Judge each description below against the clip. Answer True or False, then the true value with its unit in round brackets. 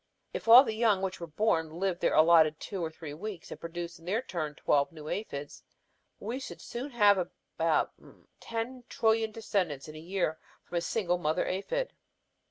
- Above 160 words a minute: True (180 wpm)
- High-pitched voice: False (180 Hz)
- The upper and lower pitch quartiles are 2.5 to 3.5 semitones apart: False (5.3 semitones)